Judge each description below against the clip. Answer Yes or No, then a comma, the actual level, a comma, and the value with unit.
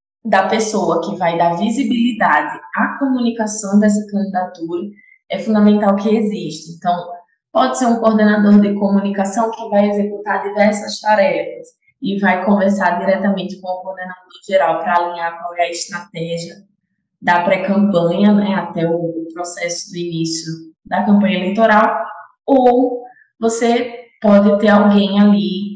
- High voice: Yes, high, 200 Hz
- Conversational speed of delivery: Yes, average, 135 wpm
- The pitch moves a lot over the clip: No, average, 3.4 semitones